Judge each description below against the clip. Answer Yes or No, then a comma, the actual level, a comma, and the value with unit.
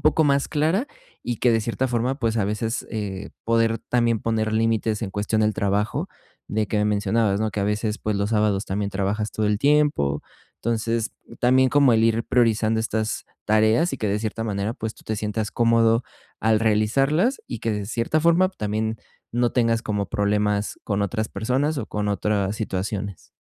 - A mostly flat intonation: Yes, narrow, 2.0 semitones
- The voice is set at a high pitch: No, low, 110 Hz